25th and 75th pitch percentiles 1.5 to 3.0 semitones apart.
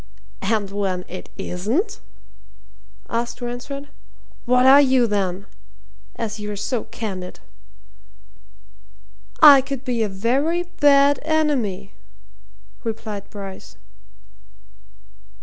No: wide, 5.5 semitones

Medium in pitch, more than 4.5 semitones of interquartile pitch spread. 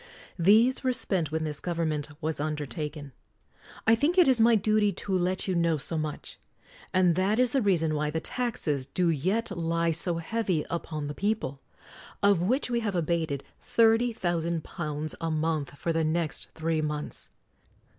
Yes: medium, 170 Hz; average, 5.0 semitones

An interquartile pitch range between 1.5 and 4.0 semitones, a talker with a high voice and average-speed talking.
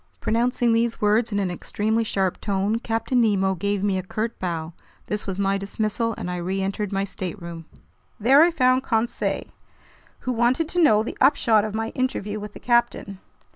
Yes: average, 3.3 semitones; high, 215 Hz; average, 175 wpm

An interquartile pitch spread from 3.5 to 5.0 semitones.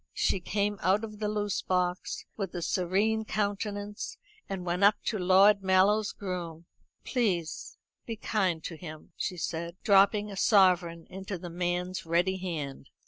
No: average, 2.7 semitones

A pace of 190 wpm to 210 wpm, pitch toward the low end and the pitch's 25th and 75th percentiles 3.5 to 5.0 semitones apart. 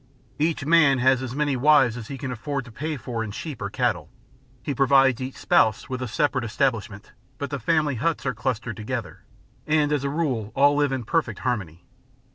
Yes: average, 200 wpm; low, 130 Hz; average, 3.8 semitones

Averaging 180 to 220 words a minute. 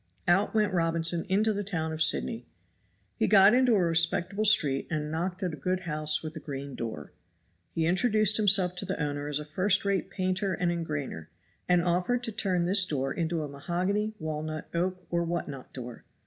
Yes: average, 190 wpm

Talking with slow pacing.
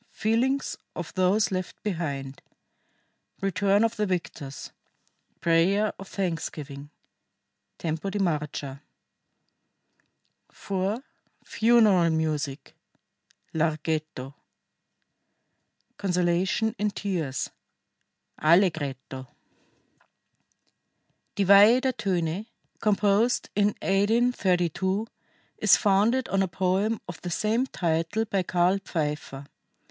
Yes: slow, 85 wpm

